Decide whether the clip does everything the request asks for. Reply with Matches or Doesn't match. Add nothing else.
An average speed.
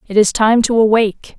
Doesn't match